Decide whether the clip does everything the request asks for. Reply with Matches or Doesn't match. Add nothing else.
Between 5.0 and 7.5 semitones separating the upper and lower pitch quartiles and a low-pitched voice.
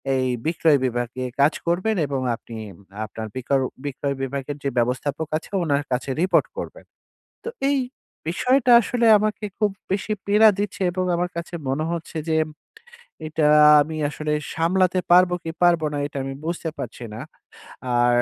Doesn't match